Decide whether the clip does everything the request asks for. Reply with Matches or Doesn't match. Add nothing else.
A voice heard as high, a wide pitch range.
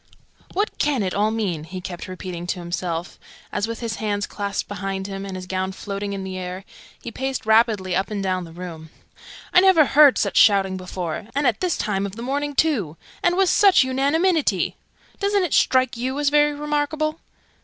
Matches